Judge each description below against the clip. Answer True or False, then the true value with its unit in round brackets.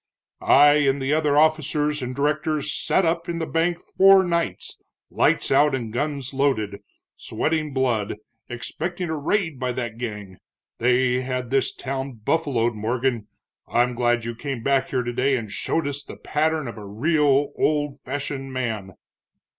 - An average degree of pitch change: True (3.8 semitones)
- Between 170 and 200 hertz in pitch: False (135 Hz)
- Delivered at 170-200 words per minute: False (155 wpm)